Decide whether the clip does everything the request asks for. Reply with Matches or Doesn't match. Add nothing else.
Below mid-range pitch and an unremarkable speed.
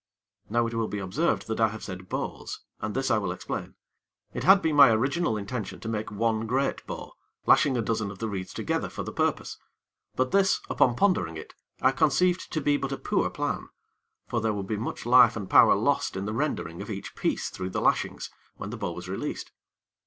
Doesn't match